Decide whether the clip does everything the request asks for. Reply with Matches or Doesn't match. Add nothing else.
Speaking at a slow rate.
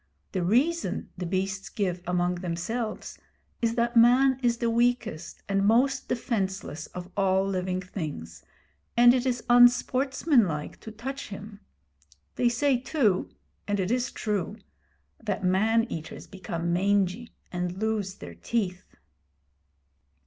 Matches